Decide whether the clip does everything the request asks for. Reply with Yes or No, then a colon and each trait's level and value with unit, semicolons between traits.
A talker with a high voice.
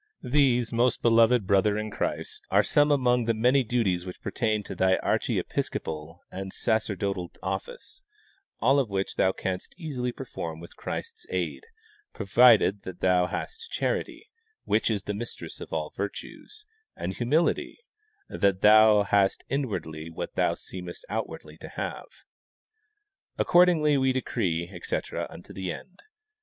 No: low, 110 Hz